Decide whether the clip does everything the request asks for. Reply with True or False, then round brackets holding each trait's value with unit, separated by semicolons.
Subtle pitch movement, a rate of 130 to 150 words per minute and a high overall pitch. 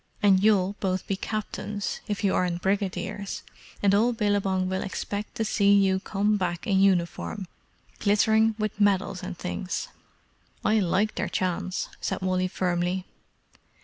True (1.9 semitones; 145 wpm; 195 Hz)